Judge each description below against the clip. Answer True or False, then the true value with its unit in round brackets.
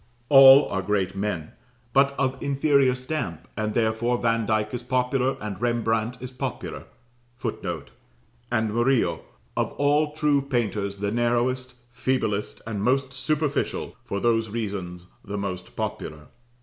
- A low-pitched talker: True (120 Hz)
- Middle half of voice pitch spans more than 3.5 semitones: True (4.3 semitones)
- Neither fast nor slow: False (130 wpm)